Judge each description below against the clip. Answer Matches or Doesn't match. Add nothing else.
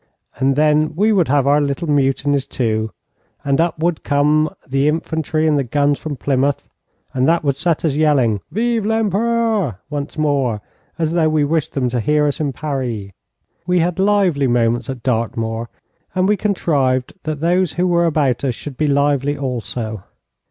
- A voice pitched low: Doesn't match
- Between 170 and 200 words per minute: Matches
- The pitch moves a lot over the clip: Doesn't match